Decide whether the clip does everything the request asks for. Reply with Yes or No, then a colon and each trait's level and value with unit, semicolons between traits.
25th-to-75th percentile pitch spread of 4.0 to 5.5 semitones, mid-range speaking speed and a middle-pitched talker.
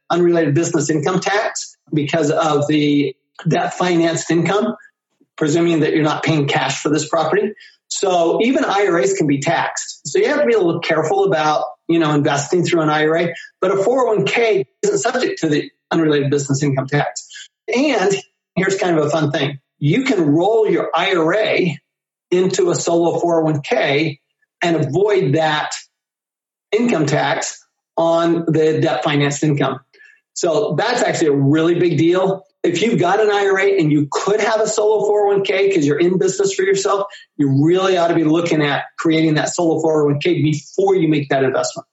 Yes: average, 4.3 semitones; average, 170 wpm; medium, 165 Hz